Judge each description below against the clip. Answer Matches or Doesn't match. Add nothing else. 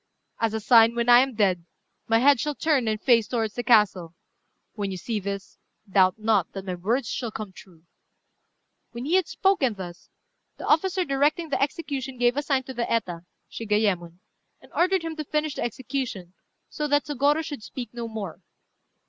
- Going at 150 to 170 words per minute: Doesn't match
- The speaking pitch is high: Matches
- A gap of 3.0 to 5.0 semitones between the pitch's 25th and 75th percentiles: Doesn't match